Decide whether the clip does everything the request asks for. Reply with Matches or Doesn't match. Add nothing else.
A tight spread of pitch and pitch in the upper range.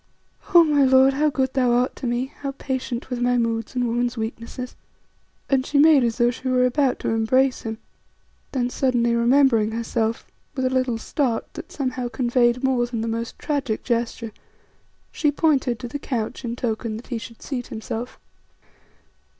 Matches